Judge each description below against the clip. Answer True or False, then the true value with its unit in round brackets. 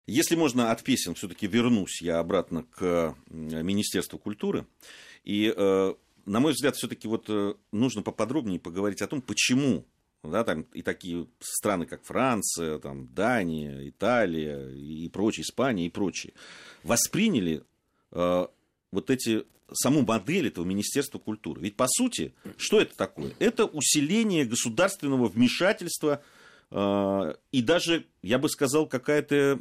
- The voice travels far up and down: True (8.5 semitones)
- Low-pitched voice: True (105 Hz)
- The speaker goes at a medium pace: True (130 wpm)